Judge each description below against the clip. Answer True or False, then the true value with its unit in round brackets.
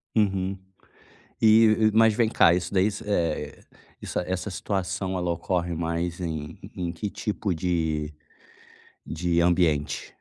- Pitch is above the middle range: False (90 Hz)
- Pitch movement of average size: True (3.1 semitones)